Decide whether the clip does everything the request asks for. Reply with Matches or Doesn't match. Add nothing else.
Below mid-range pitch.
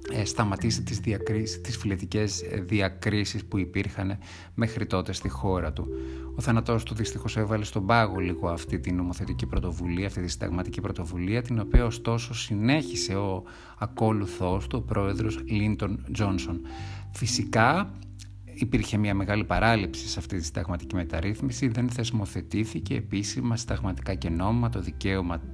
Matches